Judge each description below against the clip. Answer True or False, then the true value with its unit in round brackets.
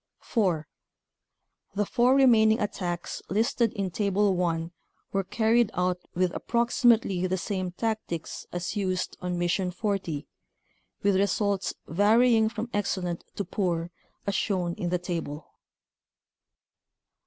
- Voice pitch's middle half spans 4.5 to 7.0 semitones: False (3.6 semitones)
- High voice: True (195 Hz)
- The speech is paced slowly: True (120 wpm)